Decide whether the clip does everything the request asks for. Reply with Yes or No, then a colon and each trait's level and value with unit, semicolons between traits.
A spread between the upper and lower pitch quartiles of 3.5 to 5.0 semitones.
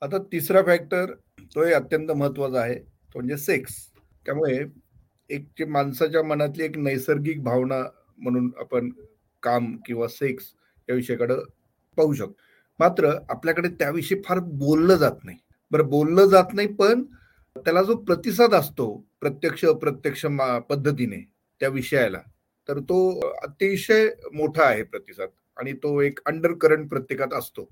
No: wide, 5.4 semitones